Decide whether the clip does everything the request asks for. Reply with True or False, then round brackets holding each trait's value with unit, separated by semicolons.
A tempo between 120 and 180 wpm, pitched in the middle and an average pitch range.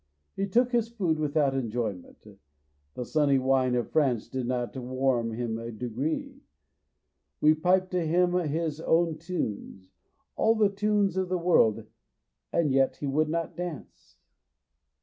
False (145 wpm; 155 Hz; 6.0 semitones)